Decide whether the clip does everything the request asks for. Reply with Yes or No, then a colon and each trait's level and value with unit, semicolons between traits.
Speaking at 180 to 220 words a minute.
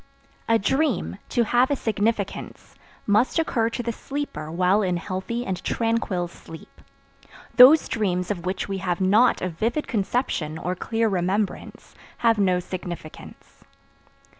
No: average, 140 wpm